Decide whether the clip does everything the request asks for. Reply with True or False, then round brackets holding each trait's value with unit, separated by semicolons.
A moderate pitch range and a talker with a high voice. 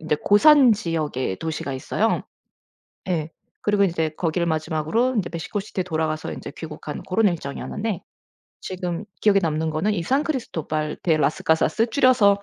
False (4.9 semitones; 170 Hz)